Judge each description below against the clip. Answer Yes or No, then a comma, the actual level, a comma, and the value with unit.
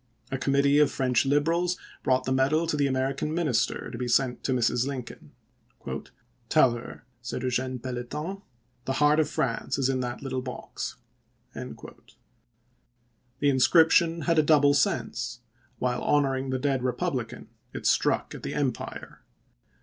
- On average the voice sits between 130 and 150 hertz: Yes, low, 135 Hz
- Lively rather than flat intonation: No, average, 2.7 semitones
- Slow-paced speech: No, average, 150 wpm